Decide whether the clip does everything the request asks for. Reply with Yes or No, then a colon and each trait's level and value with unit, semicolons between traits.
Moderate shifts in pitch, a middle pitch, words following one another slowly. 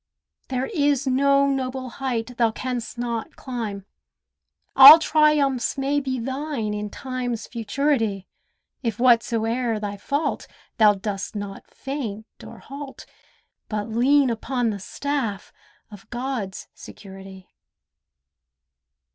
No: average, 4.1 semitones; high, 245 Hz; slow, 110 wpm